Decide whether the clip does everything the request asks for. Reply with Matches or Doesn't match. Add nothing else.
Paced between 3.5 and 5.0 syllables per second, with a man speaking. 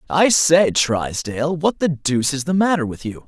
Matches